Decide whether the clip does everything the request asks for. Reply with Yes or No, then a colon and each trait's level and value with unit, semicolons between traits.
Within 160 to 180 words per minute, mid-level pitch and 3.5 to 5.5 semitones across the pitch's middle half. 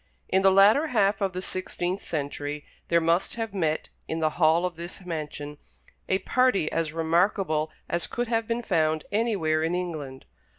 Yes: average, 170 wpm; medium, 175 Hz; average, 3.9 semitones